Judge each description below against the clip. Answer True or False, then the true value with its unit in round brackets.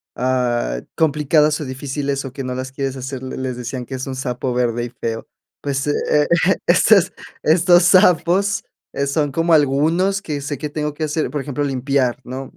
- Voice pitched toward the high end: False (140 Hz)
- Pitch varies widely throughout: False (3.3 semitones)